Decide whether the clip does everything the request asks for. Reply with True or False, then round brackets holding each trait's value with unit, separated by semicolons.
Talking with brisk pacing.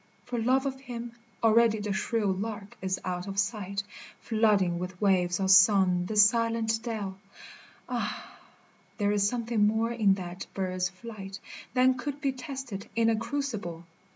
False (155 wpm)